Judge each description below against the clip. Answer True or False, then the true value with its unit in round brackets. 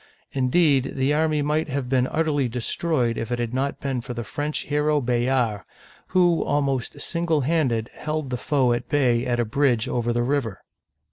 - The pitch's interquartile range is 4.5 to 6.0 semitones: False (3.6 semitones)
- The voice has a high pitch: False (135 Hz)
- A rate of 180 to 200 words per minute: True (190 wpm)